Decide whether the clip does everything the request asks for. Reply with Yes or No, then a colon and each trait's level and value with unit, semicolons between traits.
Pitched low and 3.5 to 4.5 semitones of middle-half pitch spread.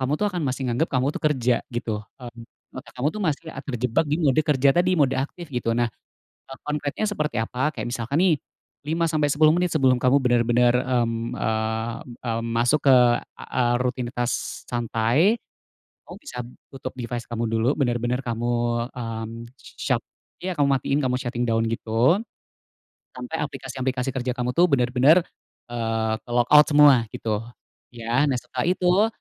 Yes: low, 125 Hz; average, 3.9 semitones